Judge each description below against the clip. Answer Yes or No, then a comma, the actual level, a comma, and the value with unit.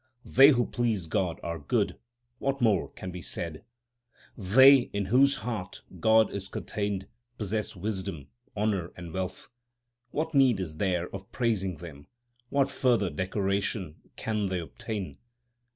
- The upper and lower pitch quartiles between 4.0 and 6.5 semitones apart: Yes, average, 4.3 semitones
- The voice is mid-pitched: No, low, 100 Hz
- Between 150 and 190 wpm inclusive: No, slow, 135 wpm